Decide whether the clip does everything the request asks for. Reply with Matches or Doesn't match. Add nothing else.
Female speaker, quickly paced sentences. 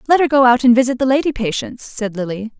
Matches